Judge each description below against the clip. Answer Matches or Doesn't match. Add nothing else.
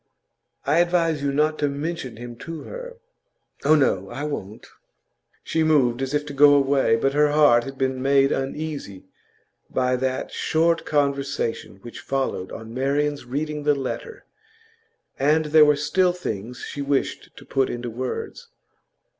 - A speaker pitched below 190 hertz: Matches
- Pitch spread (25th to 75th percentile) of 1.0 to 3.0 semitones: Matches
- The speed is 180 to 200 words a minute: Doesn't match